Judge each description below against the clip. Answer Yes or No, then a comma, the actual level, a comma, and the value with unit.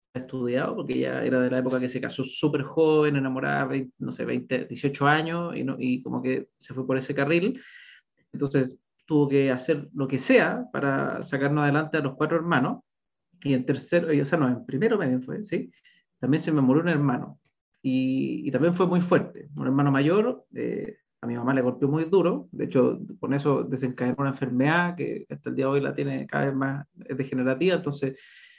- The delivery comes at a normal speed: No, fast, 205 wpm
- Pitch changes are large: No, average, 3.6 semitones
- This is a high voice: No, medium, 140 Hz